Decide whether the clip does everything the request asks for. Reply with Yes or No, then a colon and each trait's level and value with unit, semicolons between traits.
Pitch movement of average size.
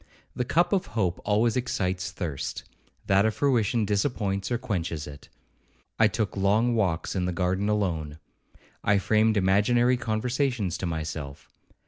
Yes: average, 4.2 semitones